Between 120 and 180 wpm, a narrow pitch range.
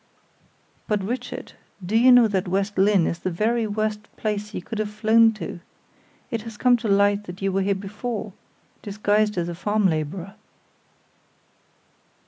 Yes: average, 160 wpm; narrow, 2.1 semitones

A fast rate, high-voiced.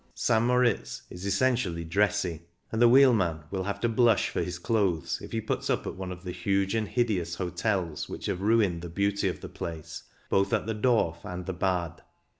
No: fast, 210 wpm; very low, 95 Hz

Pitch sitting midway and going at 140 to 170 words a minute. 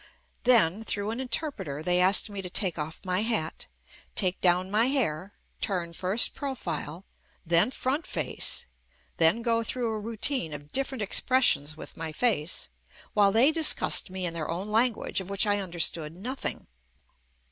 No: high, 200 Hz; average, 160 wpm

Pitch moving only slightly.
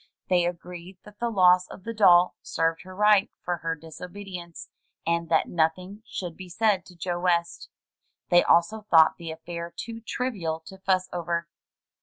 Yes: narrow, 2.3 semitones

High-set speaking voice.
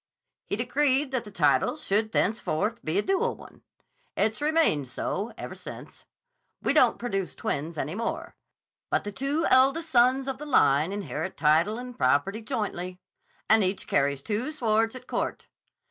Yes: high, 220 Hz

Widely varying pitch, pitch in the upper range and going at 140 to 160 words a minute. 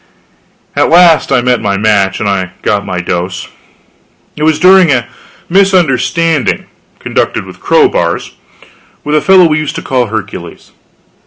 No: wide, 8.5 semitones; low, 130 Hz; average, 145 wpm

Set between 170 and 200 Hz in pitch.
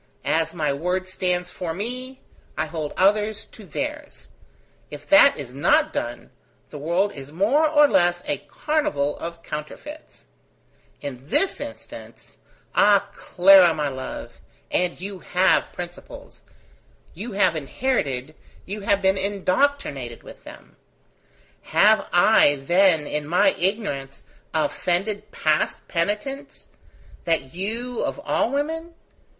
Yes: medium, 185 Hz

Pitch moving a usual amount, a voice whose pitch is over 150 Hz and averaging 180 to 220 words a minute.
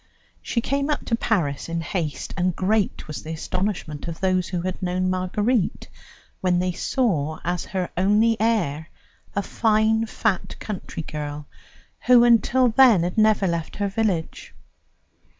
No: average, 4.6 semitones; medium, 185 Hz; average, 150 wpm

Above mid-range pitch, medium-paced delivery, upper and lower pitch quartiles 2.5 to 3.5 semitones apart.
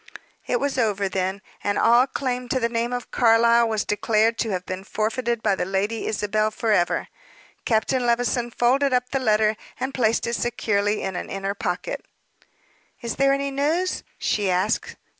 Yes: high, 230 Hz; average, 170 wpm; average, 3.1 semitones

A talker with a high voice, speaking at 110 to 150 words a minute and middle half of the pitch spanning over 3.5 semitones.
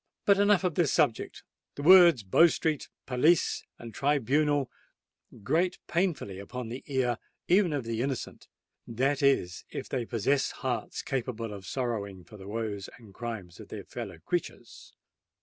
No: low, 125 Hz; average, 140 wpm; average, 5.0 semitones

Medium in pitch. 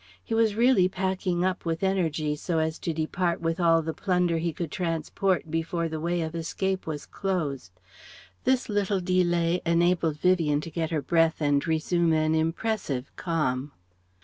Yes: medium, 170 Hz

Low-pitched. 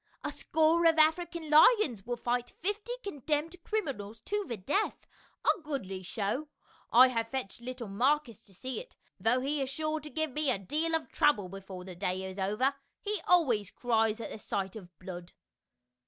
No: very high, 255 Hz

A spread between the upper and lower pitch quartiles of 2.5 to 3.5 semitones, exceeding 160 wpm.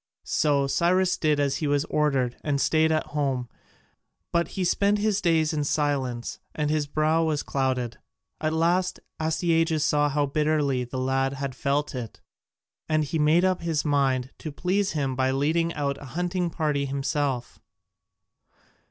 No: average, 2.9 semitones; average, 155 wpm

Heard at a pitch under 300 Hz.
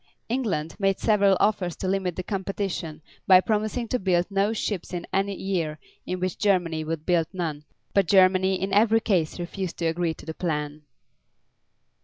Yes: medium, 185 Hz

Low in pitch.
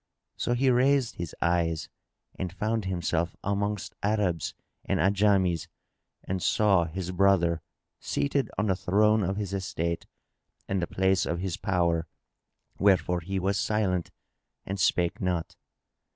Yes: very low, 95 Hz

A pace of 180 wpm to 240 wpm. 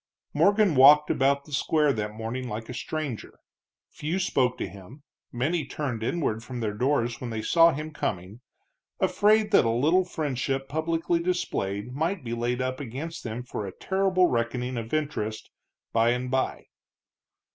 No: average, 160 wpm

